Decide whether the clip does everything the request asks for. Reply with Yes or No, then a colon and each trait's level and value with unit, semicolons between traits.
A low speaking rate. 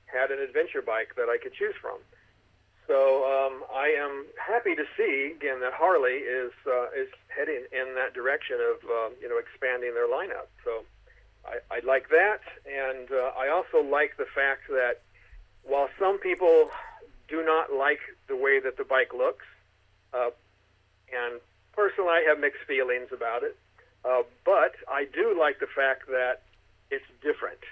No: average, 165 wpm